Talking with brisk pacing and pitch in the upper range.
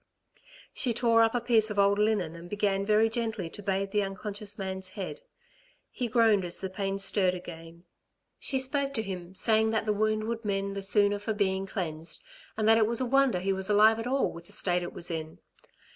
Yes: fast, 215 wpm; high, 205 Hz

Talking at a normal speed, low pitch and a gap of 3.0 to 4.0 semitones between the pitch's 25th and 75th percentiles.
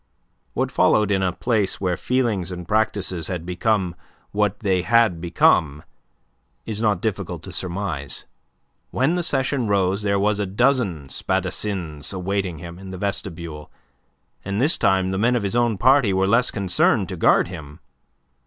Yes: average, 160 wpm; very low, 95 Hz; average, 3.5 semitones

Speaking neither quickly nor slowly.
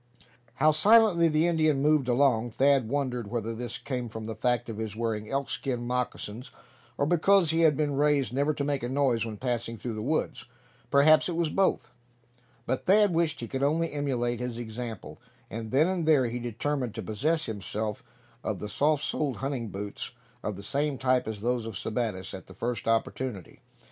Yes: average, 190 wpm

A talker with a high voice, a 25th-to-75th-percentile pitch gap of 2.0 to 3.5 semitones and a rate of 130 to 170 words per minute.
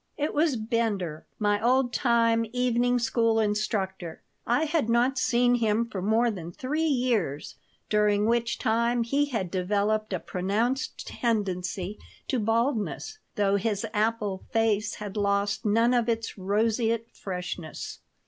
Yes: high, 225 Hz; average, 2.8 semitones; slow, 135 wpm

